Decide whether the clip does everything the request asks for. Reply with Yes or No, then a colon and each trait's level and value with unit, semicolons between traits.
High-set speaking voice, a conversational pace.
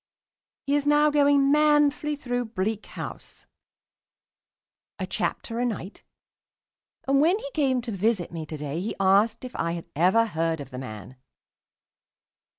Yes: high, 230 Hz; average, 155 wpm